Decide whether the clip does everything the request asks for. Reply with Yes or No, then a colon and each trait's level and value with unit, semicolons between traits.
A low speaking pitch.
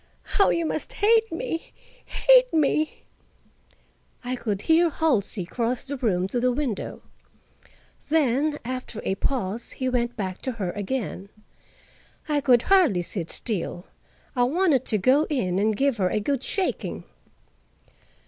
No: very high, 255 Hz